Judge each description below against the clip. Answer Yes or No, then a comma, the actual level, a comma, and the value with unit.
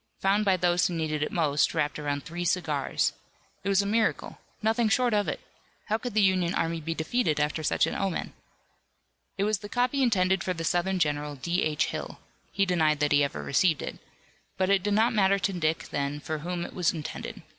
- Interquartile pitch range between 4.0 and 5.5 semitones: Yes, average, 4.3 semitones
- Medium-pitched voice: Yes, medium, 175 Hz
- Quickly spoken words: Yes, fast, 210 wpm